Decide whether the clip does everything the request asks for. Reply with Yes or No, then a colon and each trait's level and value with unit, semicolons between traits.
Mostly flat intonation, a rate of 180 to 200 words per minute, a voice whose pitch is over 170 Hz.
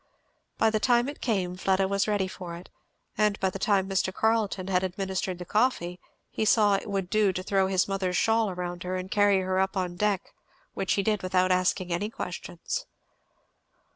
Yes: narrow, 2.2 semitones; average, 195 wpm; high, 190 Hz